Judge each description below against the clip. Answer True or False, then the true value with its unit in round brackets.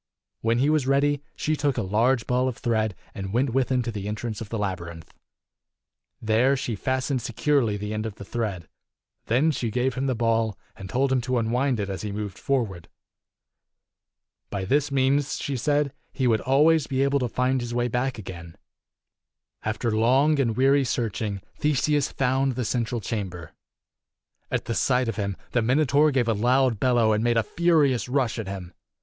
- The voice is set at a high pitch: False (120 Hz)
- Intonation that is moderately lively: True (3.8 semitones)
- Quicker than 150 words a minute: True (185 wpm)